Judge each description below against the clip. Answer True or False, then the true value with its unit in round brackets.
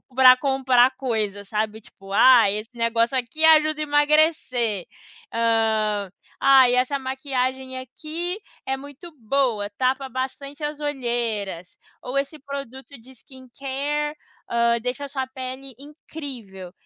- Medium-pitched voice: False (260 Hz)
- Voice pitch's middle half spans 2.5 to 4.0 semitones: True (3.4 semitones)